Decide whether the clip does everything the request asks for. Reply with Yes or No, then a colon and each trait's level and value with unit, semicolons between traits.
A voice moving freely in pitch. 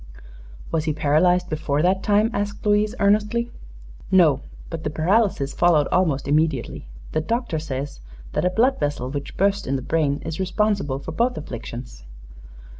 Yes: wide, 5.8 semitones